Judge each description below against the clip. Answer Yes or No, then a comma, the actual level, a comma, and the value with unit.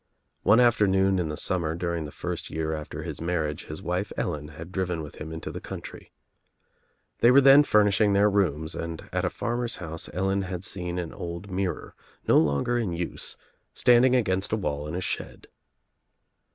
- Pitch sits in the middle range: No, very low, 90 Hz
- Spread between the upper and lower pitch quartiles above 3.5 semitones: Yes, average, 4.1 semitones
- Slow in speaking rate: No, average, 180 wpm